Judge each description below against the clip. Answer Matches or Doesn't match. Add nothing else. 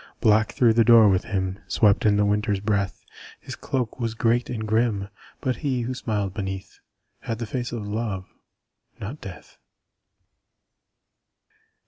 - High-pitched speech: Doesn't match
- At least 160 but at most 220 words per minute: Doesn't match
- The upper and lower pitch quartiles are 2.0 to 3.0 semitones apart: Matches